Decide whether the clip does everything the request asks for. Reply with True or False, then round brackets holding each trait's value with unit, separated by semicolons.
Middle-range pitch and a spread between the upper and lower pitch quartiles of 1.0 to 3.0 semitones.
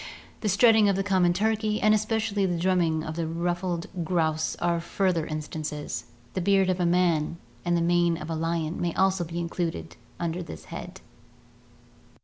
True (175 Hz; 2.6 semitones)